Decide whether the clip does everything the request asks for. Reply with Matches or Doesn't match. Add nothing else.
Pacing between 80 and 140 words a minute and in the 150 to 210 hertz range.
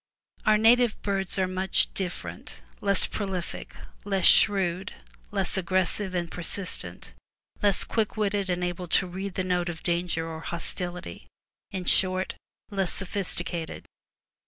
Matches